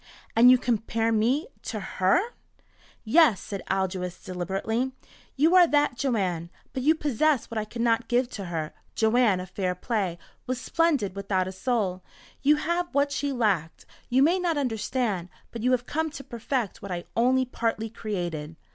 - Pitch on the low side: No, high, 230 Hz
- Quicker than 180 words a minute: No, average, 170 wpm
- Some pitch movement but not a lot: No, wide, 5.8 semitones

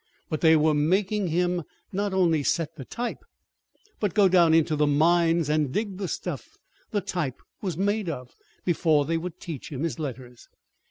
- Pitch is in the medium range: Yes, medium, 165 Hz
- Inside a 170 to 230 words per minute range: Yes, average, 175 wpm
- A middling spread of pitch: Yes, average, 3.6 semitones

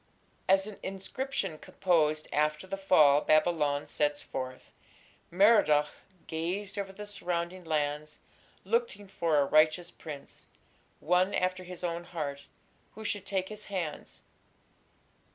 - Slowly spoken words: Yes, slow, 125 wpm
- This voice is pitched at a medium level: Yes, medium, 175 Hz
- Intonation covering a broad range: No, average, 4.2 semitones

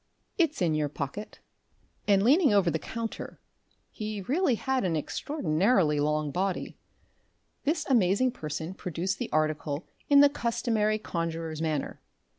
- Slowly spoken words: Yes, slow, 130 wpm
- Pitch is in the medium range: No, high, 195 Hz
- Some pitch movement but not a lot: No, wide, 7.3 semitones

